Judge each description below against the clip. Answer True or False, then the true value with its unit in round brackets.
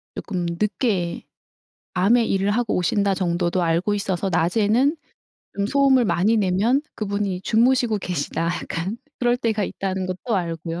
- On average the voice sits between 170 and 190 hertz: False (200 Hz)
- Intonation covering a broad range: False (4.0 semitones)